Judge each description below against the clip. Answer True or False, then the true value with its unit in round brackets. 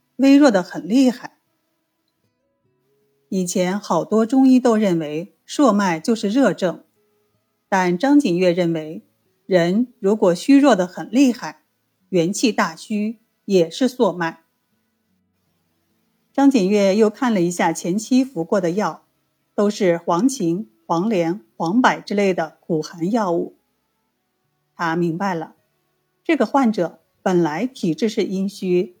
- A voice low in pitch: False (190 Hz)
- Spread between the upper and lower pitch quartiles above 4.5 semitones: True (5.1 semitones)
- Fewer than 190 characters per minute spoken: True (180 characters per minute)